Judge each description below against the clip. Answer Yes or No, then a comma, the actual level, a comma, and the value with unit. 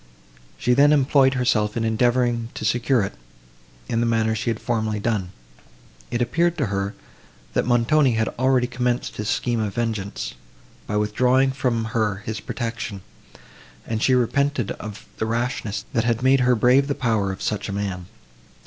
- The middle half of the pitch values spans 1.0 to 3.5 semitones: Yes, average, 2.8 semitones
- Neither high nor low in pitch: No, low, 115 Hz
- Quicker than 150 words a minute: Yes, average, 165 wpm